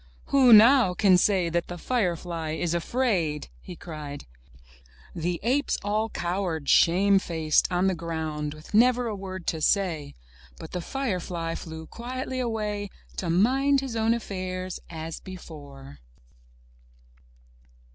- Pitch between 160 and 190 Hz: Yes, medium, 185 Hz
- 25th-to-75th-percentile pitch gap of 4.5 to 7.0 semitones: Yes, average, 5.1 semitones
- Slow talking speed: Yes, slow, 130 wpm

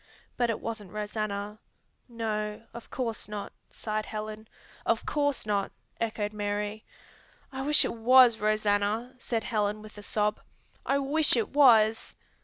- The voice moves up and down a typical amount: No, narrow, 2.0 semitones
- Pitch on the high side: Yes, high, 215 Hz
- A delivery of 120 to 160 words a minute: Yes, average, 140 wpm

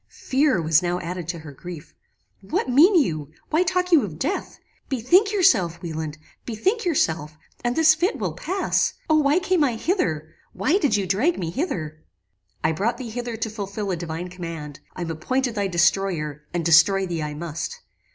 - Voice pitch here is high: Yes, high, 195 Hz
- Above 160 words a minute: Yes, average, 180 wpm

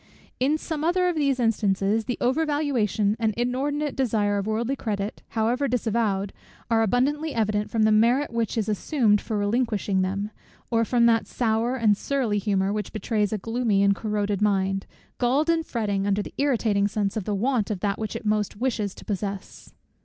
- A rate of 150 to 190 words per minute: Yes, average, 185 wpm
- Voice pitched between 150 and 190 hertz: No, high, 220 Hz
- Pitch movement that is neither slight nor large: Yes, average, 3.5 semitones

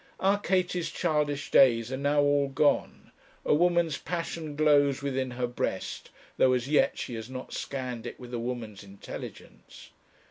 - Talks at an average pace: Yes, average, 155 wpm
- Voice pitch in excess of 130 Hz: Yes, medium, 140 Hz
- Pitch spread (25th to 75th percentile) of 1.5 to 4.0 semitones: Yes, average, 3.6 semitones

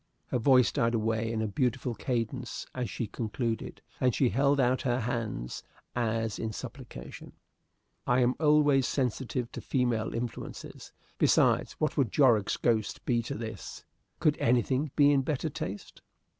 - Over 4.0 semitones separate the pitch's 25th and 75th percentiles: No, average, 2.7 semitones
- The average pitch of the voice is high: No, low, 120 Hz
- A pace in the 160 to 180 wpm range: No, average, 150 wpm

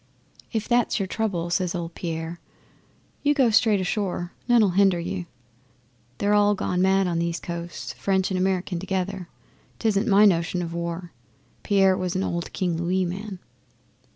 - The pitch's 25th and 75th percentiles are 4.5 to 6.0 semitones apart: No, narrow, 2.6 semitones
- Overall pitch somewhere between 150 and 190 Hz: Yes, medium, 185 Hz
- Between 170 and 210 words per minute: No, average, 155 wpm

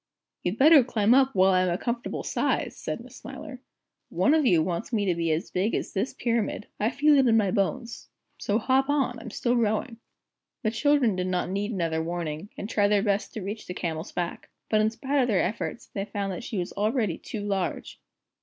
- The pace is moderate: No, fast, 215 wpm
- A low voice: No, high, 215 Hz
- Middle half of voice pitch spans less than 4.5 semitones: No, average, 4.8 semitones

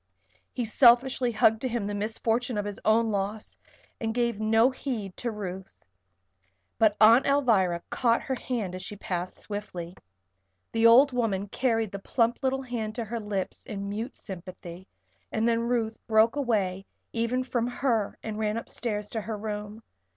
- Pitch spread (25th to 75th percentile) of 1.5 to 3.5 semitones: Yes, narrow, 2.6 semitones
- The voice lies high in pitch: Yes, high, 220 Hz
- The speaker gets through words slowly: No, average, 165 wpm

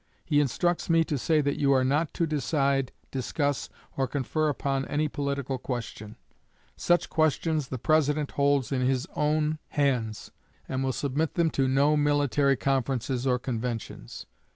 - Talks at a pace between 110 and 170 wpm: Yes, average, 155 wpm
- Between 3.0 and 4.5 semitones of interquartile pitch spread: No, narrow, 2.5 semitones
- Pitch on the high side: No, medium, 140 Hz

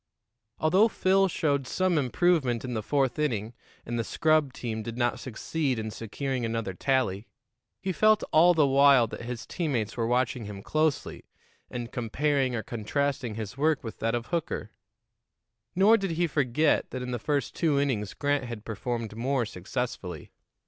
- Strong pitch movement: No, average, 4.8 semitones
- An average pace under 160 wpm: No, average, 165 wpm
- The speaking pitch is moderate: No, low, 130 Hz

